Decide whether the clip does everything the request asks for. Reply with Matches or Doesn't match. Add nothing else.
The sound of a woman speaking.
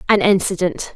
Matches